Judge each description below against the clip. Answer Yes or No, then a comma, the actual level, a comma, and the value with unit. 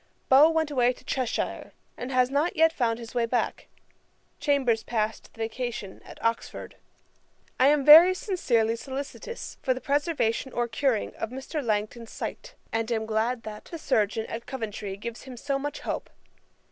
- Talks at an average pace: Yes, average, 165 wpm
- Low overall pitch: No, high, 245 Hz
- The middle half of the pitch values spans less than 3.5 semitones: No, average, 3.9 semitones